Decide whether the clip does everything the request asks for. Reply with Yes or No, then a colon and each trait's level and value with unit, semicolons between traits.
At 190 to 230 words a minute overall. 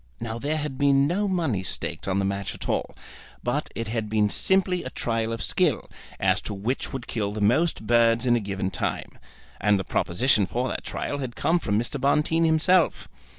Yes: average, 200 wpm